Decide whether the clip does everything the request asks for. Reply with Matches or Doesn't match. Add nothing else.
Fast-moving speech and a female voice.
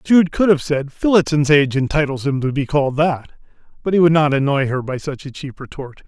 Doesn't match